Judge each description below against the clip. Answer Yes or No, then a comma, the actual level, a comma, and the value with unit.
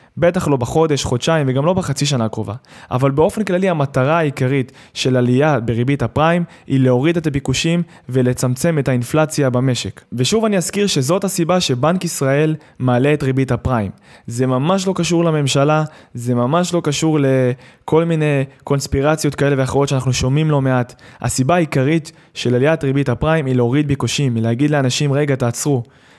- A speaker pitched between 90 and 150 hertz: Yes, medium, 140 Hz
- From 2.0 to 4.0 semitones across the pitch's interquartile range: Yes, average, 3.7 semitones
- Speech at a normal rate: No, fast, 155 wpm